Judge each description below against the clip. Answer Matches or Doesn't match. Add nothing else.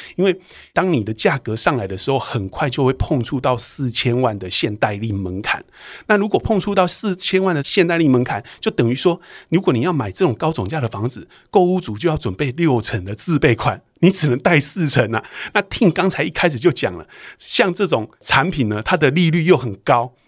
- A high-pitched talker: Doesn't match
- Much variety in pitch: Matches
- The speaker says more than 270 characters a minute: Matches